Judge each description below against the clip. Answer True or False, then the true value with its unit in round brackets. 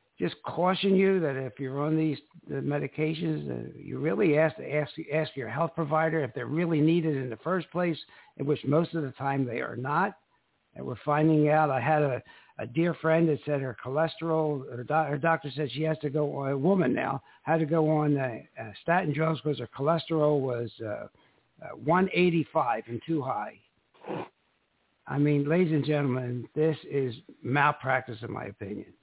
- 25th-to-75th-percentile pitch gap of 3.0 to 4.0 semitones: True (3.4 semitones)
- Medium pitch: True (150 Hz)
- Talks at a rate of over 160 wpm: True (190 wpm)